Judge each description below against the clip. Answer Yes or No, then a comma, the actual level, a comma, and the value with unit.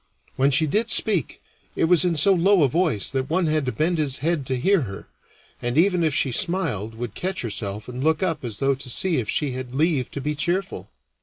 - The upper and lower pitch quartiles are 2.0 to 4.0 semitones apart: No, wide, 5.4 semitones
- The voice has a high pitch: No, medium, 150 Hz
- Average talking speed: No, fast, 230 wpm